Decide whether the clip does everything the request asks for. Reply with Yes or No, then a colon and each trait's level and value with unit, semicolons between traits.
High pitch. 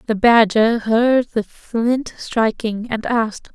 Yes: high, 225 Hz